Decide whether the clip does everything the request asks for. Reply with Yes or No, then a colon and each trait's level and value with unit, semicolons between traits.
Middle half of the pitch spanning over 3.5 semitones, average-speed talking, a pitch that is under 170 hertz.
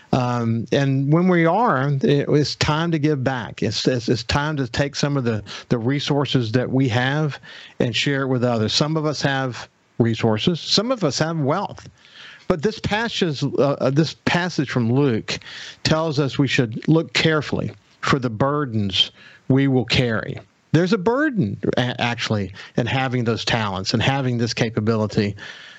Yes: average, 4.2 semitones; average, 170 wpm; low, 135 Hz